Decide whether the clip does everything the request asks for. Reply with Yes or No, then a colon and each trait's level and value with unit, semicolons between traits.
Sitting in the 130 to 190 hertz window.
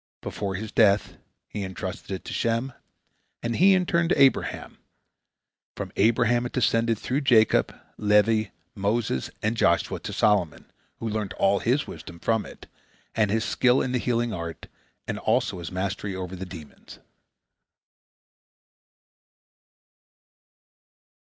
No: low, 110 Hz